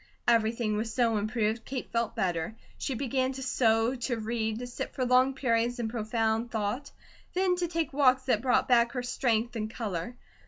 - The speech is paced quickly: No, average, 185 wpm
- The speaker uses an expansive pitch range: No, narrow, 2.6 semitones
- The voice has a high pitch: Yes, high, 235 Hz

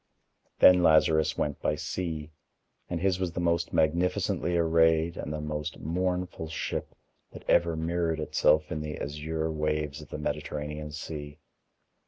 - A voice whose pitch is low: Yes, very low, 80 Hz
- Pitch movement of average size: No, narrow, 1.9 semitones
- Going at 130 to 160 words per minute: Yes, average, 145 wpm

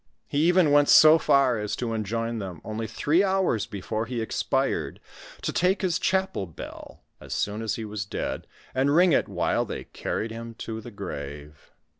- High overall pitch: No, low, 115 Hz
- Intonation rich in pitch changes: Yes, wide, 6.4 semitones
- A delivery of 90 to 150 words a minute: No, average, 180 wpm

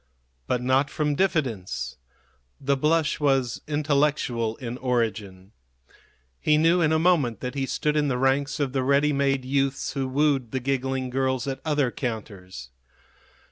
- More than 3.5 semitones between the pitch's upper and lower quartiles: No, average, 2.9 semitones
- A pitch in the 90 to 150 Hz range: Yes, low, 135 Hz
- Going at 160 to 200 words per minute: No, average, 150 wpm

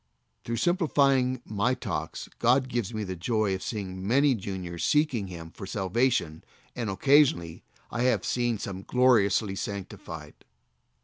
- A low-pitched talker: Yes, low, 110 Hz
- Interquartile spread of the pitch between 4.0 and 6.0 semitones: Yes, average, 5.1 semitones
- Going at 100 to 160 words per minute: Yes, slow, 135 wpm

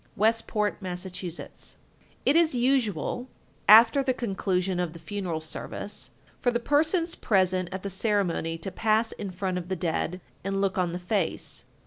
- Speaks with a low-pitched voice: No, high, 195 Hz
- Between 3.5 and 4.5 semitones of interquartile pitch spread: Yes, average, 4.0 semitones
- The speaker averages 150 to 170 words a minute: Yes, average, 160 wpm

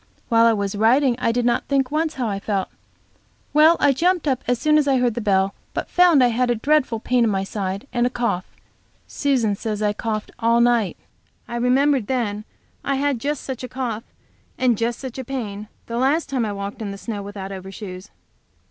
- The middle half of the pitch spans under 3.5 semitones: No, average, 4.2 semitones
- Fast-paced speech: Yes, fast, 215 wpm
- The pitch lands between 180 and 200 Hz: No, high, 235 Hz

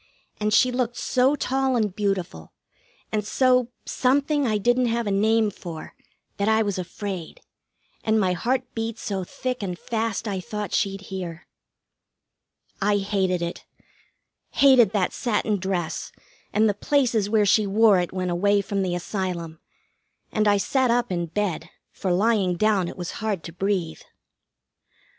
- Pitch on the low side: No, high, 205 Hz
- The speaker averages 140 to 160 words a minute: Yes, average, 155 wpm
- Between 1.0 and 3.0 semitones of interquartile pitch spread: No, average, 3.6 semitones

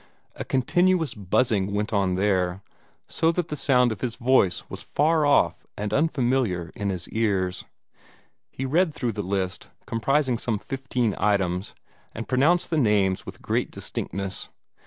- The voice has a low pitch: Yes, low, 115 Hz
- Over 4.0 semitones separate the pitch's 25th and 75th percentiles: Yes, wide, 5.6 semitones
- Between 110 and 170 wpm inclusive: Yes, average, 150 wpm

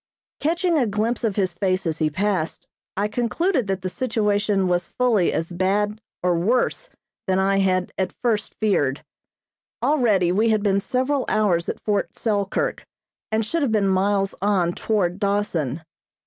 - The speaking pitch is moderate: No, high, 205 Hz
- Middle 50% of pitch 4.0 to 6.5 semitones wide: No, average, 3.1 semitones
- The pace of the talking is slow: No, average, 160 wpm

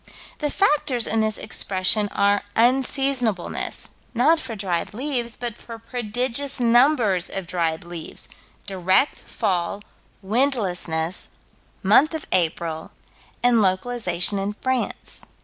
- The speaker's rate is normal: No, slow, 110 wpm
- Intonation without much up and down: No, average, 5.1 semitones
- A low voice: No, high, 220 Hz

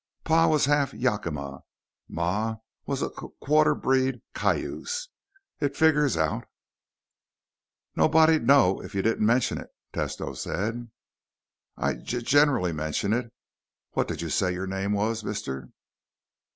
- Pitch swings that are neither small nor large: No, wide, 7.2 semitones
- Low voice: Yes, low, 115 Hz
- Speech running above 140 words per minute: No, slow, 135 wpm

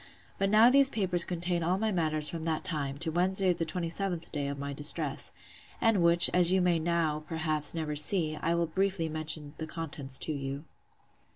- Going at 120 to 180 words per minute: No, average, 190 wpm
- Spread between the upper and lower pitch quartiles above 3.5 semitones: No, average, 2.7 semitones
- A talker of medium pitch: Yes, medium, 165 Hz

